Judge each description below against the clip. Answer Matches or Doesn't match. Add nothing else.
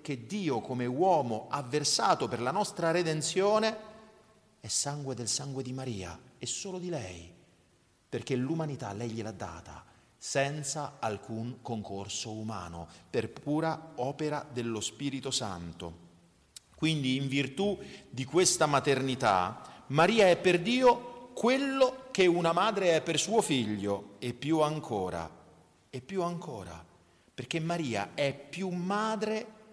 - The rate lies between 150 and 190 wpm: Doesn't match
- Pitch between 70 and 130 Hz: Doesn't match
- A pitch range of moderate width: Doesn't match